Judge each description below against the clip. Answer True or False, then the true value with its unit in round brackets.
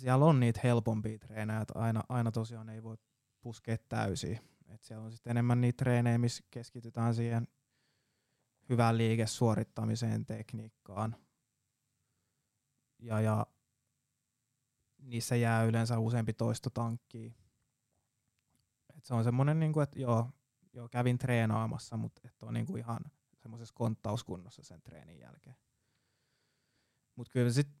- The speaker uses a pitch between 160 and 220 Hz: False (115 Hz)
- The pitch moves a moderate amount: False (2.0 semitones)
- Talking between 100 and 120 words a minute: True (115 wpm)